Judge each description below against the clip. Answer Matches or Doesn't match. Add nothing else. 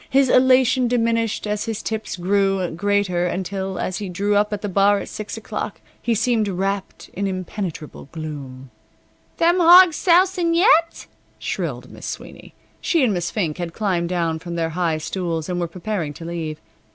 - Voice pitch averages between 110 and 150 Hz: Doesn't match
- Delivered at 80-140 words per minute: Doesn't match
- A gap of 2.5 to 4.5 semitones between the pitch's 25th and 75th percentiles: Doesn't match